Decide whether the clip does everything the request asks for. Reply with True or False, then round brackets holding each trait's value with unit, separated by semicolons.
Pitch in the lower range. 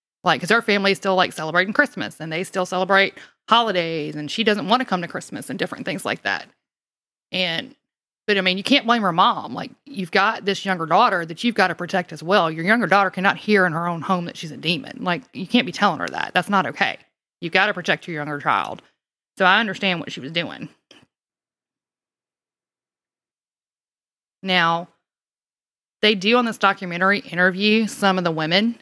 False (190 Hz)